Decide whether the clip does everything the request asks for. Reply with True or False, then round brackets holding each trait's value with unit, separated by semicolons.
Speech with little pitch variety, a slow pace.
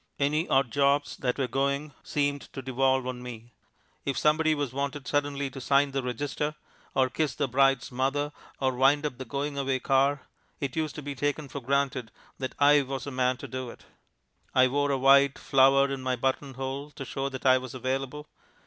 False (1.6 semitones; 200 wpm)